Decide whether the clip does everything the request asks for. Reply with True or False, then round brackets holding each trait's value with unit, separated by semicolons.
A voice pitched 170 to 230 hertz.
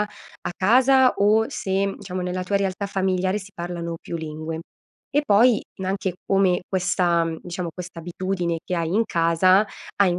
True (185 Hz)